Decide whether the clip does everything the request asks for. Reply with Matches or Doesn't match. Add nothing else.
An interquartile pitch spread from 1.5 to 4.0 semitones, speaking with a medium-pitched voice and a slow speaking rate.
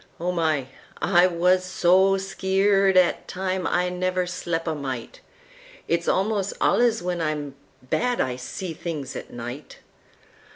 Matches